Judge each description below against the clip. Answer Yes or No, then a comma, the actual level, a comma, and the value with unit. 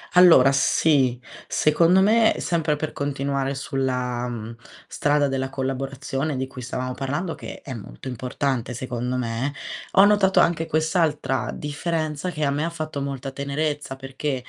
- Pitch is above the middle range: No, medium, 140 Hz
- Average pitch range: Yes, average, 3.1 semitones